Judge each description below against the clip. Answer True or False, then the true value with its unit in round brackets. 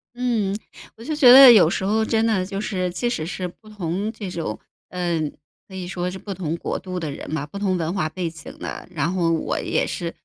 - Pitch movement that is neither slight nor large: True (4.1 semitones)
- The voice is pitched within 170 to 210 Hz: True (185 Hz)